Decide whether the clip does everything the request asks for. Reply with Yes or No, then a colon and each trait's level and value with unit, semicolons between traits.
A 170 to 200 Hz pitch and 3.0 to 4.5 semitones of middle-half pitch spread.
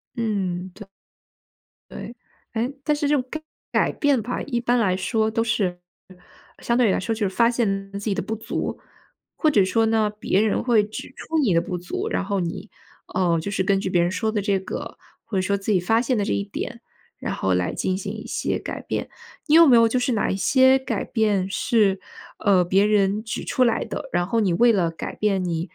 No: high, 210 Hz; average, 3.6 semitones